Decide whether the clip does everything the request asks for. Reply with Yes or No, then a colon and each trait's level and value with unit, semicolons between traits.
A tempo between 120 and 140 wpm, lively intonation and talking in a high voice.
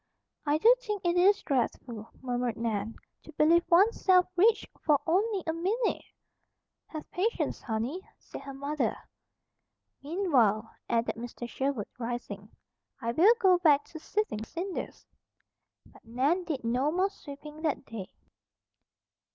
Yes: slow, 135 wpm; wide, 7.2 semitones; very high, 300 Hz